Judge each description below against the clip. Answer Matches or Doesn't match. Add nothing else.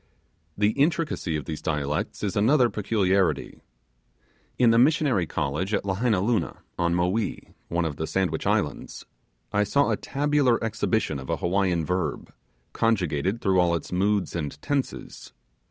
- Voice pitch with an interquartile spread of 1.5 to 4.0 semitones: Doesn't match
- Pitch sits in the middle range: Doesn't match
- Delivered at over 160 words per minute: Doesn't match